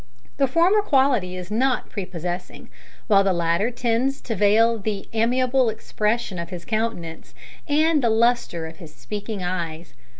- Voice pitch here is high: Yes, high, 220 Hz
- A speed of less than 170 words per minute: Yes, average, 145 wpm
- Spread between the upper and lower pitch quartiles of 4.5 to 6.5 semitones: Yes, wide, 5.4 semitones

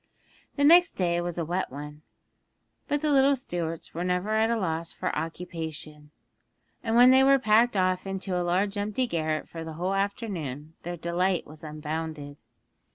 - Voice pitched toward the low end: No, medium, 180 Hz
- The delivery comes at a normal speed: Yes, average, 170 wpm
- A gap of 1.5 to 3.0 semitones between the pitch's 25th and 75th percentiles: No, average, 5.1 semitones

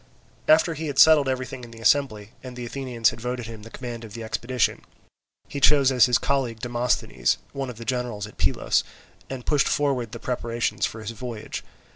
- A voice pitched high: No, low, 125 Hz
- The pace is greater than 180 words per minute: Yes, average, 195 wpm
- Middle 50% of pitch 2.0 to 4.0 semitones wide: Yes, average, 2.8 semitones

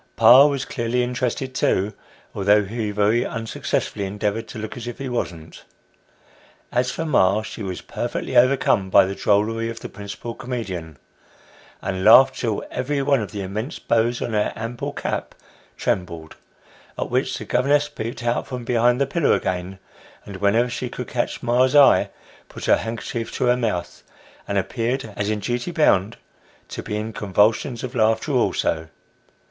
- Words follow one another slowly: No, average, 165 wpm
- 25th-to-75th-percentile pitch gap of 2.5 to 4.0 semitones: Yes, average, 3.4 semitones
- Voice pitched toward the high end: No, low, 115 Hz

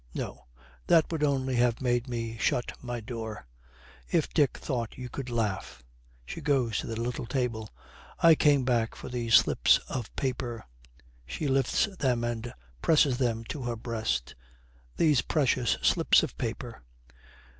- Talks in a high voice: No, low, 120 Hz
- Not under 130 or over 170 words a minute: Yes, average, 150 wpm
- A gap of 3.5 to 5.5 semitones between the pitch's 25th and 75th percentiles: No, narrow, 2.6 semitones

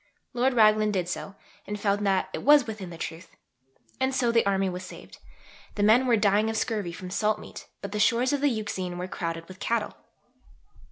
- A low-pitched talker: No, high, 210 Hz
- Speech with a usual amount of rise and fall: Yes, average, 3.7 semitones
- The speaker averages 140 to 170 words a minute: No, fast, 205 wpm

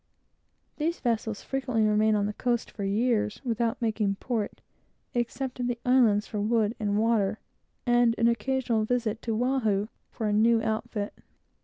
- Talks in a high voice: Yes, high, 225 Hz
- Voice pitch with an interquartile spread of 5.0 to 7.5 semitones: No, narrow, 2.4 semitones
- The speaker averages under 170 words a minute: Yes, average, 155 wpm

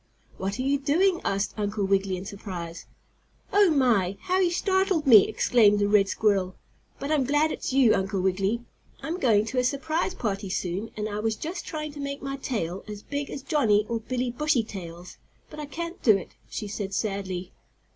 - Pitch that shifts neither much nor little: No, wide, 6.5 semitones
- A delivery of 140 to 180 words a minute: No, average, 190 wpm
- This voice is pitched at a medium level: No, high, 225 Hz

